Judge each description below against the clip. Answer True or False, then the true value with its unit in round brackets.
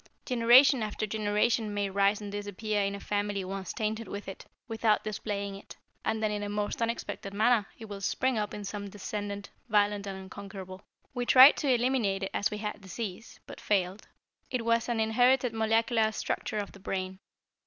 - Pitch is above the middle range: True (210 Hz)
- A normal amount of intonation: False (2.1 semitones)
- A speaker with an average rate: True (185 wpm)